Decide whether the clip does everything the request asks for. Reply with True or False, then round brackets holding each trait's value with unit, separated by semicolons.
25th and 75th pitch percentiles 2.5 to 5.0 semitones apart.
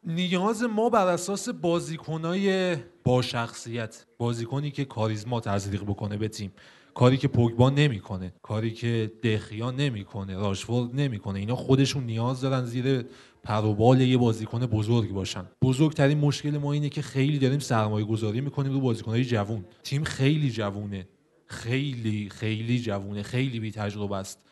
True (4.5 semitones)